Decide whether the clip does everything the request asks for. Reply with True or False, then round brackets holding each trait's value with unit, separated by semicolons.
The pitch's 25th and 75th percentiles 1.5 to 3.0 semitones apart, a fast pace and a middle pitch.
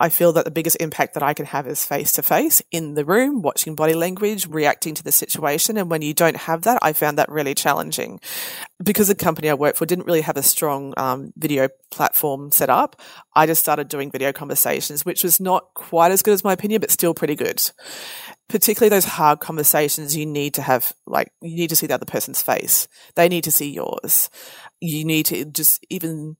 True (2.7 semitones; 220 wpm; 160 Hz)